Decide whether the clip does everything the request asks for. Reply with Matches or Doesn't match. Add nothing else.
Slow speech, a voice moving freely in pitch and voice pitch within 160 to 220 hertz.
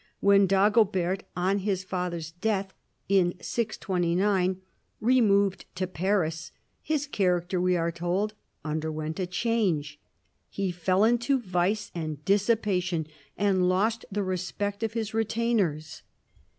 Doesn't match